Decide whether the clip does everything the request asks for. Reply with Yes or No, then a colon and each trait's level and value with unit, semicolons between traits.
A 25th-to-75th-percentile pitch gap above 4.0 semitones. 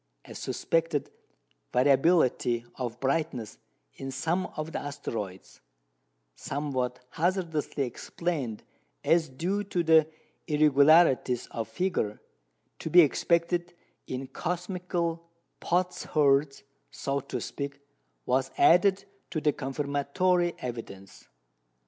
Yes: average, 4.5 semitones